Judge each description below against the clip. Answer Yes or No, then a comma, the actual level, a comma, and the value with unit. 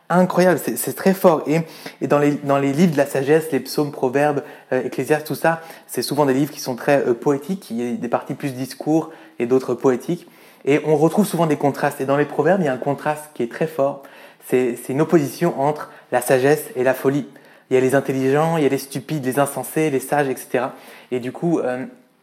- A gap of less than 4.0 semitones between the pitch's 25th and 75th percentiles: Yes, average, 2.9 semitones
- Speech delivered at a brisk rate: Yes, fast, 245 wpm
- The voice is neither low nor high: Yes, medium, 145 Hz